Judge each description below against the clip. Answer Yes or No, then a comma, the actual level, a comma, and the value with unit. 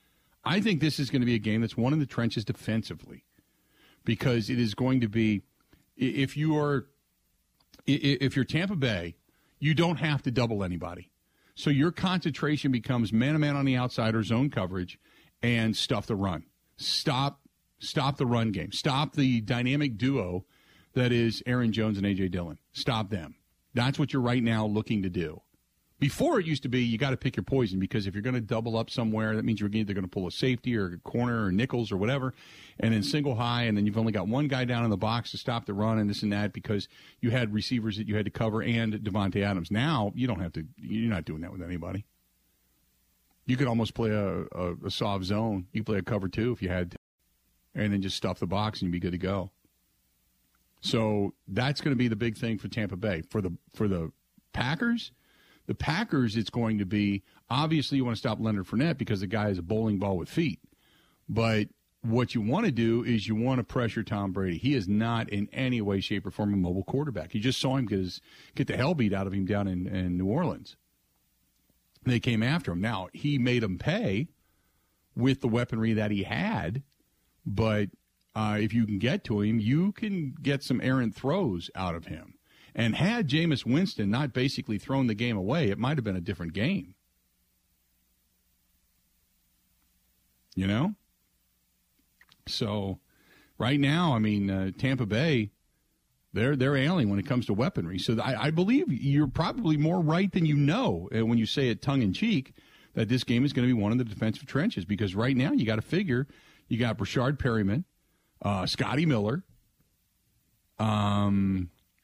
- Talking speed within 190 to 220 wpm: Yes, average, 200 wpm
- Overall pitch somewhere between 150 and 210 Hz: No, low, 110 Hz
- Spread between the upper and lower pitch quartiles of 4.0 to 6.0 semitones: Yes, average, 4.8 semitones